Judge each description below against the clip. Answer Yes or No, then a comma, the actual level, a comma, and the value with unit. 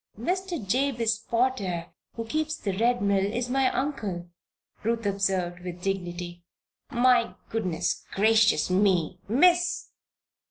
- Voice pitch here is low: No, high, 215 Hz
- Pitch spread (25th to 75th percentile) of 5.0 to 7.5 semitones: Yes, wide, 5.5 semitones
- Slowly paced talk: Yes, slow, 115 wpm